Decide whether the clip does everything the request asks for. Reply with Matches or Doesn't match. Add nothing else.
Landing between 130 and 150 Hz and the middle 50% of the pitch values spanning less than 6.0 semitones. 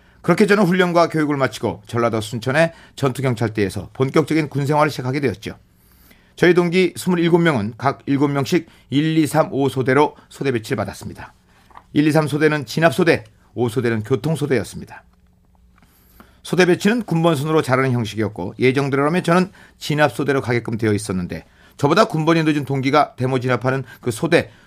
Matches